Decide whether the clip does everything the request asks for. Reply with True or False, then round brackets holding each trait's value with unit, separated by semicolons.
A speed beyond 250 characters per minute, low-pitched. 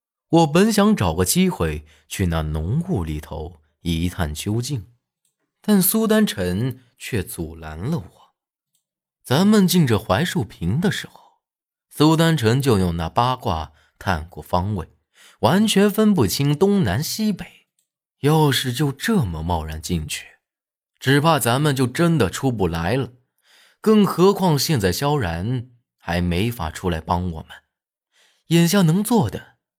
False (195 characters per minute; 130 Hz)